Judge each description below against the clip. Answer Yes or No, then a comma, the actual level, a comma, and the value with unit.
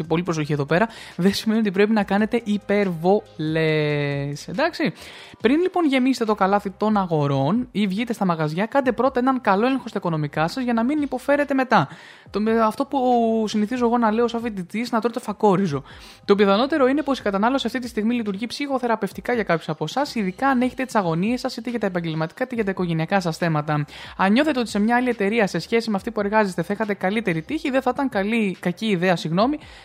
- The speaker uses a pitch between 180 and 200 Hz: No, high, 215 Hz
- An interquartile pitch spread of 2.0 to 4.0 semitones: No, average, 4.9 semitones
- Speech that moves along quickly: Yes, fast, 205 wpm